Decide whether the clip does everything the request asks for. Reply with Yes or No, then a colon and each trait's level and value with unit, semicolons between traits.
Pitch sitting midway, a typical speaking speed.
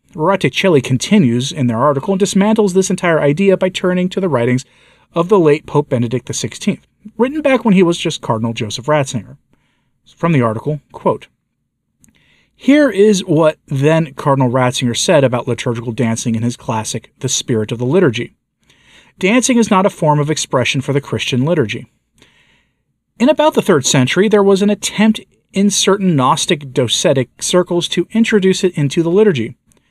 Yes: medium, 155 Hz; average, 165 wpm